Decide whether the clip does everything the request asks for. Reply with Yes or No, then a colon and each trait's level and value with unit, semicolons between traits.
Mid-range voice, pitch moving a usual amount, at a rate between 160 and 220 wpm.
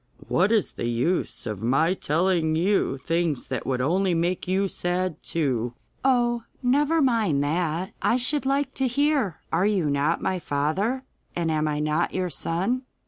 No: medium, 180 Hz; wide, 6.9 semitones; average, 165 wpm